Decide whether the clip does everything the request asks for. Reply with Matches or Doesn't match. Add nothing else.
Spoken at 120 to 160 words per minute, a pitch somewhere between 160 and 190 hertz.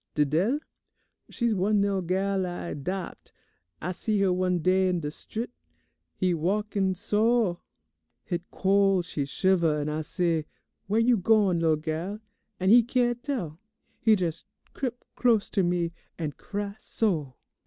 Matches